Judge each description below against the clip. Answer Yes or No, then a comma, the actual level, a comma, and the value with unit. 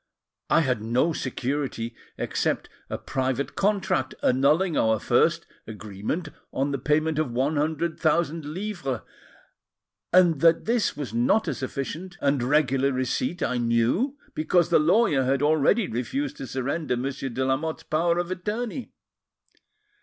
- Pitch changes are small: No, average, 4.7 semitones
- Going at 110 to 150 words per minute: Yes, average, 140 wpm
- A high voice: No, medium, 145 Hz